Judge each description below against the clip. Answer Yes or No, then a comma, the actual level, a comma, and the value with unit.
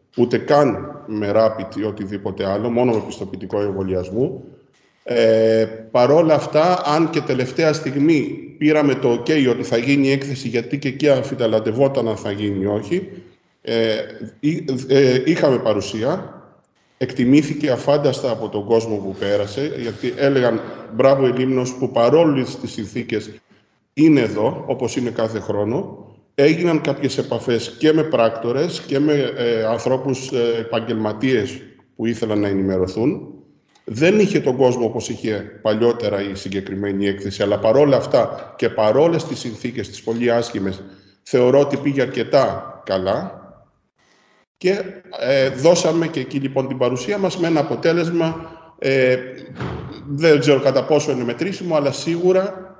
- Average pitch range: Yes, average, 4.8 semitones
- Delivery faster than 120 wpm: Yes, average, 140 wpm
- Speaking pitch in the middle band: No, low, 125 Hz